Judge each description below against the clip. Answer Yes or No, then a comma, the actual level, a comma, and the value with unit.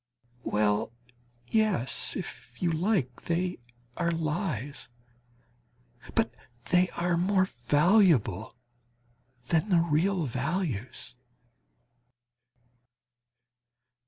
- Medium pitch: Yes, medium, 165 Hz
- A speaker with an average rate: No, slow, 70 wpm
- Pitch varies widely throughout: Yes, wide, 6.3 semitones